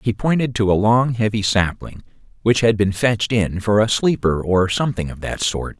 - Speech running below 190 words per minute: No, fast, 205 wpm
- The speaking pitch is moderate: No, low, 105 Hz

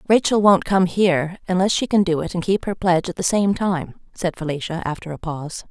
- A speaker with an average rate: No, fast, 230 wpm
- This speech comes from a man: No, female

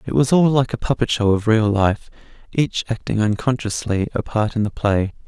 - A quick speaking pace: No, average, 195 wpm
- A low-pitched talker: Yes, low, 115 Hz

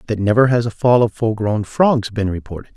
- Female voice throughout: No, male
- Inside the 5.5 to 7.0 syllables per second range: Yes, 5.6 syllables/s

